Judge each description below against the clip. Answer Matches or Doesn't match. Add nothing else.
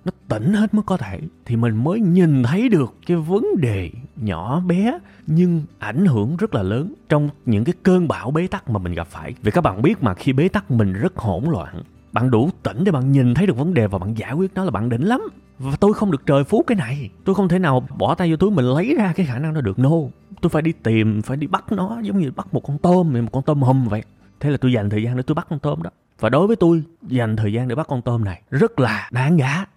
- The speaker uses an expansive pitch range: Matches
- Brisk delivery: Matches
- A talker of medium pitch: Matches